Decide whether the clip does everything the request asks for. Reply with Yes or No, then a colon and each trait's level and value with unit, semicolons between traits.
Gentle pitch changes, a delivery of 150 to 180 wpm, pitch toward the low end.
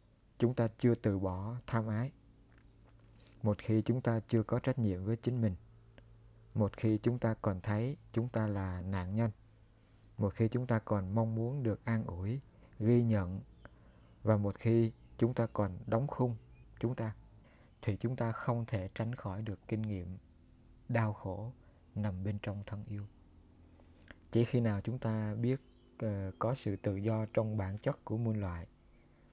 Yes: narrow, 2.2 semitones; average, 175 wpm; low, 110 Hz